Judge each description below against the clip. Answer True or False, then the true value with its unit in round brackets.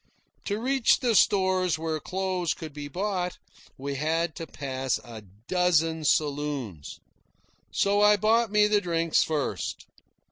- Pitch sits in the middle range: True (170 Hz)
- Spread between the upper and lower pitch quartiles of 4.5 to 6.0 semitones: True (5.2 semitones)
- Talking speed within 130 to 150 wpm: True (135 wpm)